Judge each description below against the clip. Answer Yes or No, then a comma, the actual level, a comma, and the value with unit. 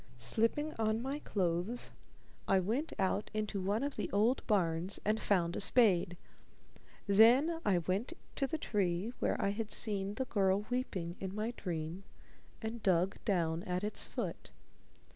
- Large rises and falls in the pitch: No, average, 3.8 semitones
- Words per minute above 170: No, average, 155 wpm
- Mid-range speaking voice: No, high, 205 Hz